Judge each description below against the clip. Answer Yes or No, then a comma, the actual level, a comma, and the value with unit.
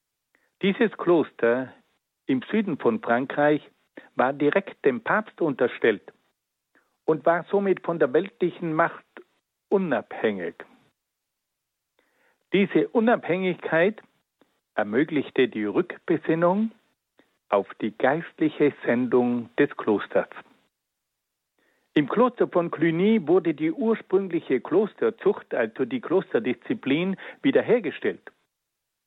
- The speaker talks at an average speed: No, slow, 85 wpm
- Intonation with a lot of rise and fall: Yes, wide, 7.2 semitones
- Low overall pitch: No, medium, 180 Hz